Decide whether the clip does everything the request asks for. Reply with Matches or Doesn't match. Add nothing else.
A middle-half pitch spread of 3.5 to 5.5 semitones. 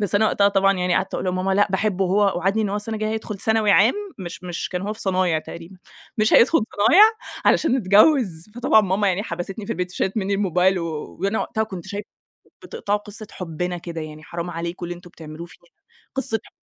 Doesn't match